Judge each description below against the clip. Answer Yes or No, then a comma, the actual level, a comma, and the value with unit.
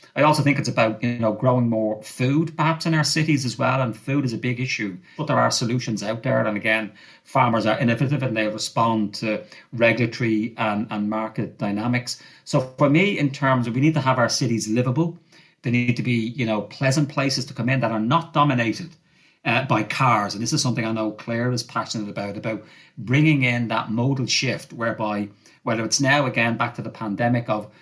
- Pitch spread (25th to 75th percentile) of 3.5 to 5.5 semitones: Yes, average, 3.8 semitones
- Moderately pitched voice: No, low, 120 Hz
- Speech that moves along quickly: Yes, fast, 215 wpm